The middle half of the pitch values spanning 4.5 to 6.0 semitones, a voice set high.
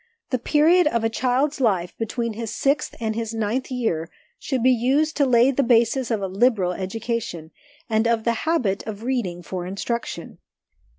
No: average, 3.7 semitones; high, 230 Hz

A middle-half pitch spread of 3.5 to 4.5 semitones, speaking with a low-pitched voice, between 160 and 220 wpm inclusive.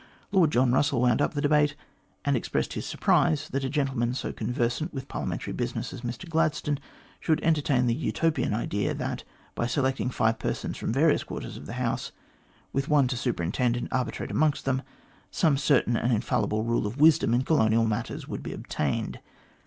Yes: average, 3.9 semitones; low, 130 Hz; average, 185 wpm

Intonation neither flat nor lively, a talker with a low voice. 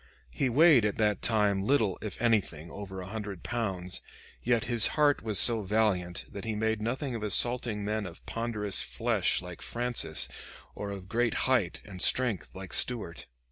Yes: average, 3.5 semitones; low, 105 Hz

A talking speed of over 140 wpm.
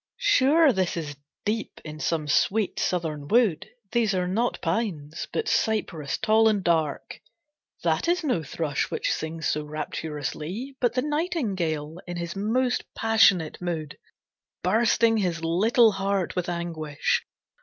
No: slow, 135 wpm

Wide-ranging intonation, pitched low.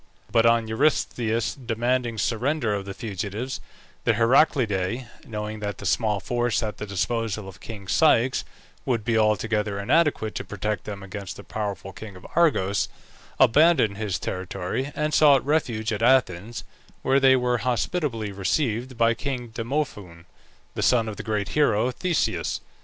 No: average, 3.8 semitones; low, 115 Hz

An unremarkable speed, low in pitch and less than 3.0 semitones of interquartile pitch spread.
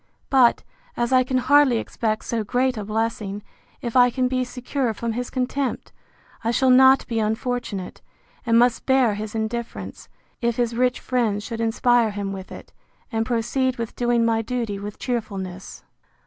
No: average, 165 wpm; high, 235 Hz; narrow, 2.4 semitones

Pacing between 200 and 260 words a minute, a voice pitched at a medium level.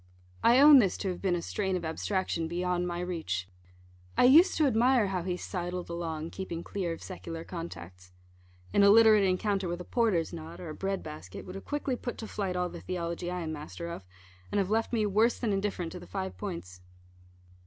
Yes: fast, 205 wpm; medium, 180 Hz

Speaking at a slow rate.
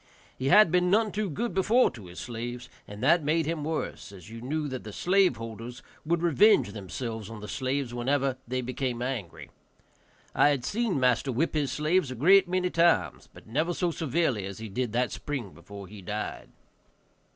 No: average, 190 wpm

